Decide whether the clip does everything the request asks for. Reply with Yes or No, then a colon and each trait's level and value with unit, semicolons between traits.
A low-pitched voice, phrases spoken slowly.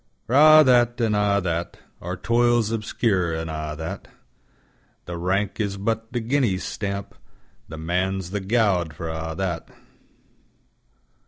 Yes: low, 100 Hz; slow, 120 wpm